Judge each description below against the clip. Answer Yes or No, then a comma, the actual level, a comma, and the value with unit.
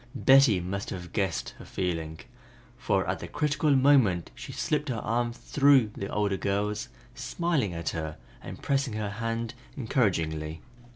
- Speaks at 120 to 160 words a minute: Yes, average, 150 wpm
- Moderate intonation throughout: No, wide, 6.8 semitones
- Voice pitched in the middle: No, low, 105 Hz